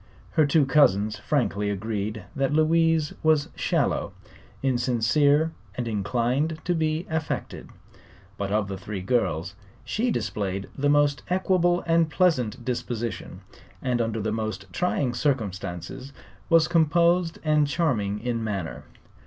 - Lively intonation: Yes, wide, 6.7 semitones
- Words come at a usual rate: No, slow, 125 wpm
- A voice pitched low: Yes, low, 130 Hz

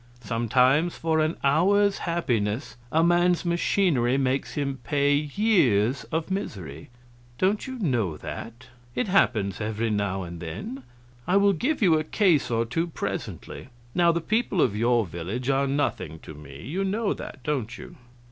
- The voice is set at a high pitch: No, medium, 140 Hz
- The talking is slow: No, average, 155 wpm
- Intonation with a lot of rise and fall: Yes, wide, 7.5 semitones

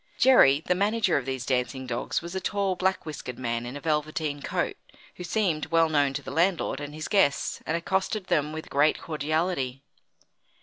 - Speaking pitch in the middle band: Yes, medium, 155 Hz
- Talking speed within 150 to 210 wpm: Yes, average, 185 wpm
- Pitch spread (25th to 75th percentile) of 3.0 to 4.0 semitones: No, average, 4.7 semitones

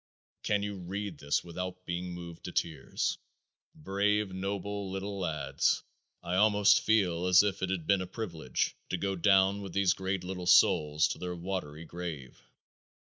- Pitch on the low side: Yes, very low, 95 Hz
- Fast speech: No, average, 160 wpm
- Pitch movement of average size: No, narrow, 2.3 semitones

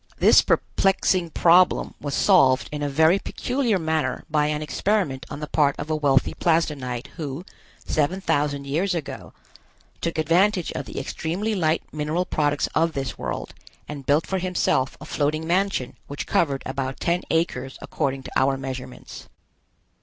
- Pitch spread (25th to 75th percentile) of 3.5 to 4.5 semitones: Yes, average, 4.0 semitones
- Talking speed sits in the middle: Yes, average, 155 wpm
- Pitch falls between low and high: Yes, medium, 155 Hz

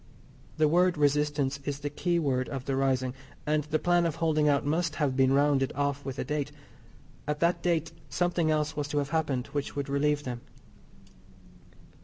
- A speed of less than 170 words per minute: No, average, 180 wpm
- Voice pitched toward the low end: No, medium, 145 Hz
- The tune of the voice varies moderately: No, narrow, 2.2 semitones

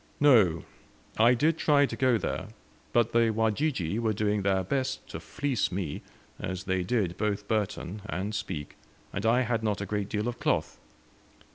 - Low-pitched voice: Yes, low, 105 Hz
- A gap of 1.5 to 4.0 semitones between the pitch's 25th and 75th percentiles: Yes, average, 3.5 semitones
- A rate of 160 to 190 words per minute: Yes, average, 170 wpm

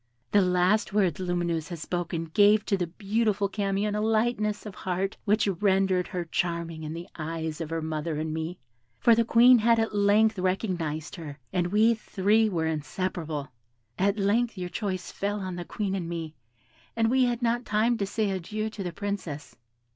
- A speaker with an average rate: Yes, average, 185 wpm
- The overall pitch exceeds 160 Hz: Yes, high, 190 Hz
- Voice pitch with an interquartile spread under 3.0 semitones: No, average, 4.0 semitones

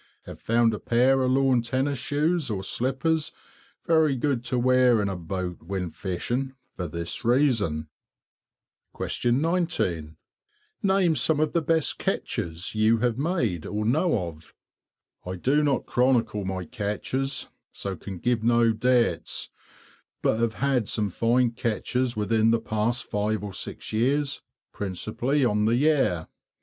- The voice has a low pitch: Yes, low, 120 Hz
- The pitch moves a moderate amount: Yes, average, 4.7 semitones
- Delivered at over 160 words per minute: No, average, 140 wpm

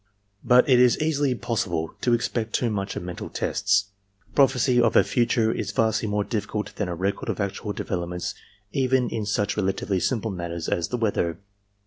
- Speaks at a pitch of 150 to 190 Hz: No, low, 105 Hz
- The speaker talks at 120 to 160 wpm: No, average, 175 wpm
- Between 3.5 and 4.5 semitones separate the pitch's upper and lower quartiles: Yes, average, 3.8 semitones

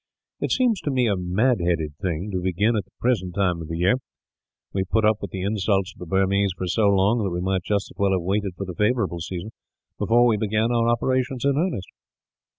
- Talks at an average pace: No, fast, 235 wpm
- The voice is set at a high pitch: No, low, 100 Hz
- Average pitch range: Yes, average, 3.8 semitones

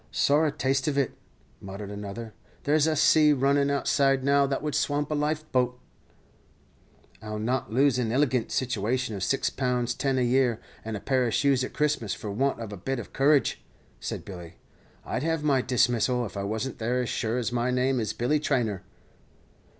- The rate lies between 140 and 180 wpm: No, average, 190 wpm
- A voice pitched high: No, low, 125 Hz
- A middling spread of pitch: Yes, average, 3.7 semitones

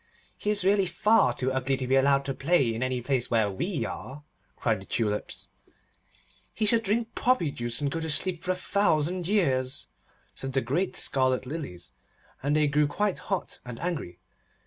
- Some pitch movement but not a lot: No, wide, 6.1 semitones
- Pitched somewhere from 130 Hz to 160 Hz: Yes, medium, 140 Hz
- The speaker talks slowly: No, average, 185 wpm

